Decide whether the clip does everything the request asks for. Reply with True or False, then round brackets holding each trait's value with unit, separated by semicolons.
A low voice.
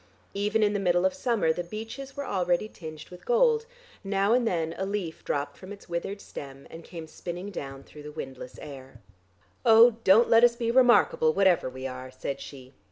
False (185 Hz)